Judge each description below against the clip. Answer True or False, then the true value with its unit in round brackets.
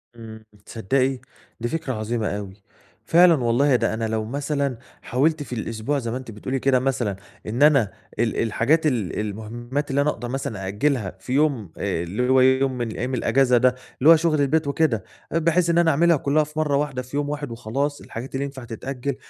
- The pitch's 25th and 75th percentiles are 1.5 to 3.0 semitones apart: False (4.1 semitones)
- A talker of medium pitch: False (130 Hz)